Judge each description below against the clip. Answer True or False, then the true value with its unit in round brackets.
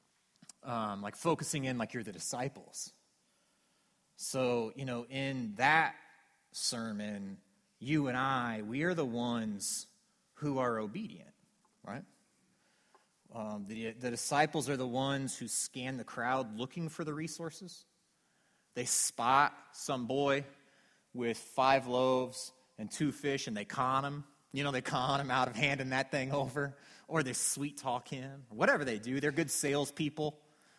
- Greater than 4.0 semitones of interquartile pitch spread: False (3.0 semitones)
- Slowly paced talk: False (150 wpm)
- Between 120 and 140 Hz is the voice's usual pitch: True (135 Hz)